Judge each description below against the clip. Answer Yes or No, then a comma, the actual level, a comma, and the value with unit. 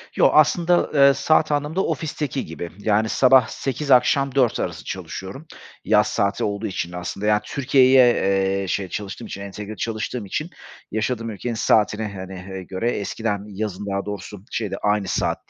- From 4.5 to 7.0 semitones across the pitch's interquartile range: Yes, average, 4.9 semitones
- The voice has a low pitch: Yes, low, 105 Hz